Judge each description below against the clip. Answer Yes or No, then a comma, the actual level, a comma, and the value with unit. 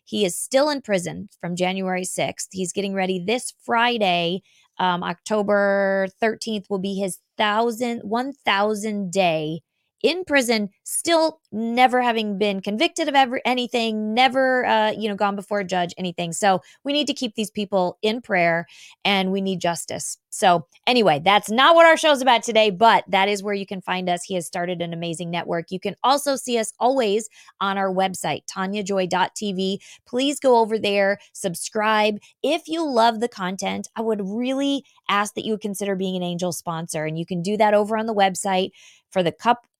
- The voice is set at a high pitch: Yes, high, 205 Hz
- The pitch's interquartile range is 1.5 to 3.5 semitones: No, average, 4.0 semitones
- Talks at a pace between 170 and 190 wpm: Yes, average, 180 wpm